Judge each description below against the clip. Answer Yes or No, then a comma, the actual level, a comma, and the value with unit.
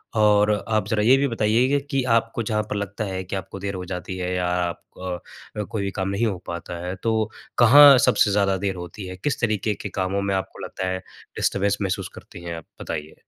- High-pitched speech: No, low, 100 Hz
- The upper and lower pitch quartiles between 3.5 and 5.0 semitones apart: No, average, 2.9 semitones